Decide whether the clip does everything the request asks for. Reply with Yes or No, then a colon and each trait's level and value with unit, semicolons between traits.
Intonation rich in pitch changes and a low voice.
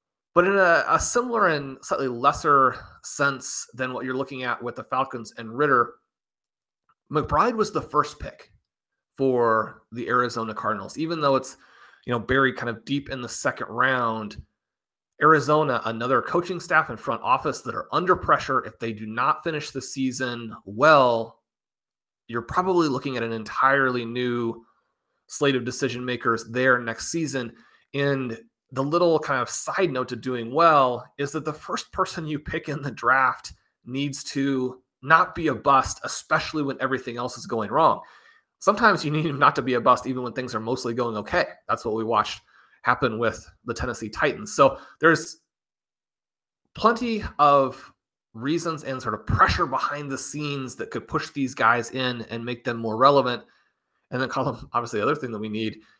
No: average, 3.8 semitones; low, 130 Hz